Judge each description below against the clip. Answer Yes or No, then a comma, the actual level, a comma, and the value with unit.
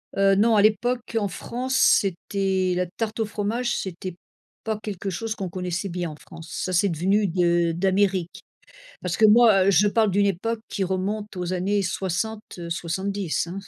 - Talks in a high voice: Yes, high, 195 Hz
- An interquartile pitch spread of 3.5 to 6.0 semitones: No, average, 2.9 semitones